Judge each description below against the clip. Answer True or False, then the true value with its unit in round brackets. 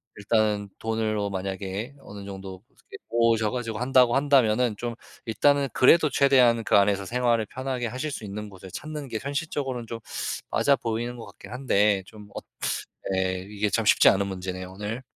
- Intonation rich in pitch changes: False (3.9 semitones)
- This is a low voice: True (110 Hz)